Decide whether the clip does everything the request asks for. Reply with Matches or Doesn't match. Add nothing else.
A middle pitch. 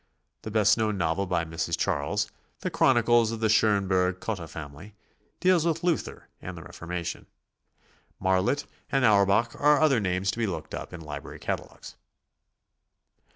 Doesn't match